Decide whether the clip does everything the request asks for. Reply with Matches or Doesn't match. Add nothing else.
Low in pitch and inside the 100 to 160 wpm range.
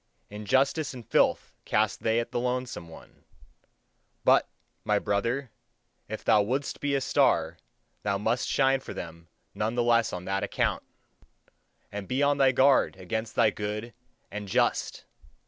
Matches